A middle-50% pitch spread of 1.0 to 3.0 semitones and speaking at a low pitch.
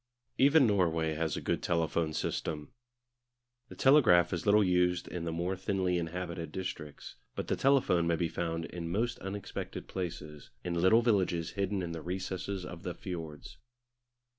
Yes: narrow, 2.6 semitones; very low, 90 Hz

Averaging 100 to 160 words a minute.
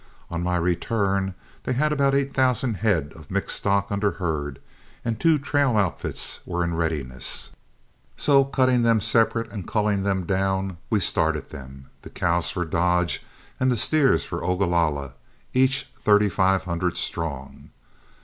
Yes: average, 150 wpm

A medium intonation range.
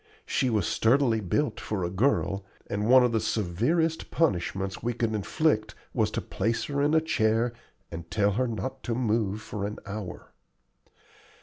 Yes: average, 4.2 semitones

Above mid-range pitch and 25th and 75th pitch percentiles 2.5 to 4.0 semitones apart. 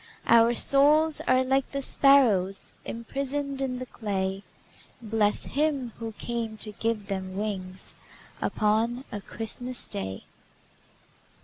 No: high, 230 Hz; average, 4.5 semitones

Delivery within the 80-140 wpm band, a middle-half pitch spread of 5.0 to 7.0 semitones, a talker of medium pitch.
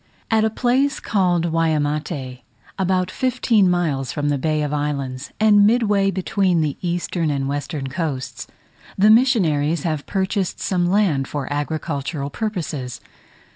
Yes: slow, 135 wpm; average, 5.3 semitones; medium, 165 Hz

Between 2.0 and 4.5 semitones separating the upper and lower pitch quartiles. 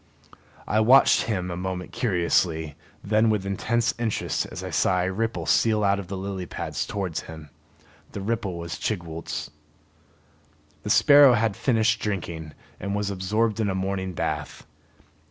Yes: average, 3.4 semitones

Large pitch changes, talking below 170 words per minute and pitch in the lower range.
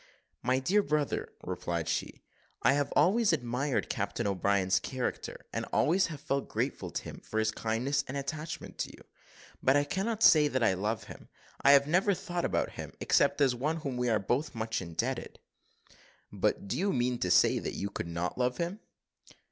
No: wide, 5.8 semitones; average, 190 wpm; low, 130 Hz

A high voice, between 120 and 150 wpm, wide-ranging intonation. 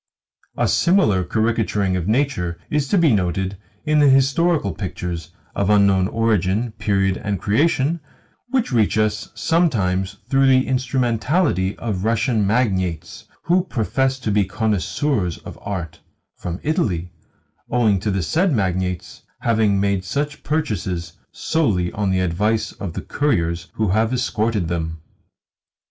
No: low, 105 Hz; slow, 135 wpm; wide, 6.0 semitones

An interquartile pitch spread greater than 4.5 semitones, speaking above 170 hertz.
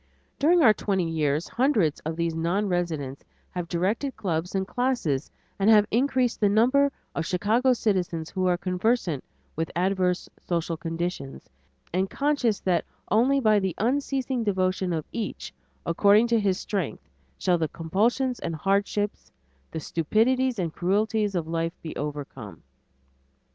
Yes: average, 5.2 semitones; high, 190 Hz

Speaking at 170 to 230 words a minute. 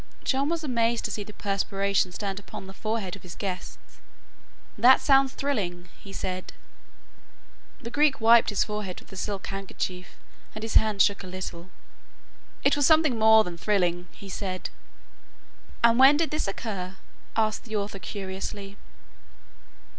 No: average, 155 wpm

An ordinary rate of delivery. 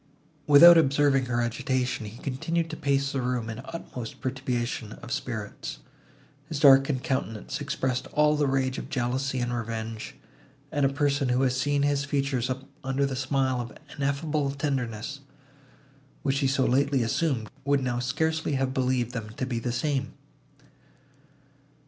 Yes: average, 155 wpm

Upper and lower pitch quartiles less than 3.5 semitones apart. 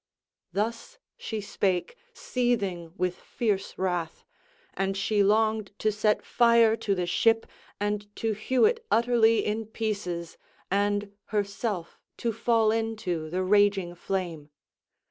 Yes: average, 3.0 semitones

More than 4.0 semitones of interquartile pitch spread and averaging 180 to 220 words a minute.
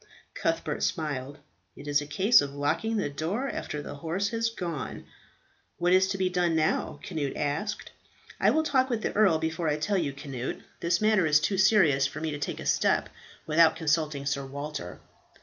Yes: average, 5.1 semitones; average, 190 wpm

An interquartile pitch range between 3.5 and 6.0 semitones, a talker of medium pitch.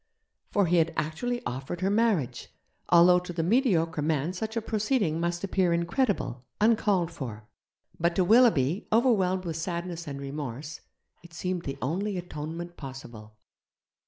Yes: average, 4.4 semitones; medium, 170 Hz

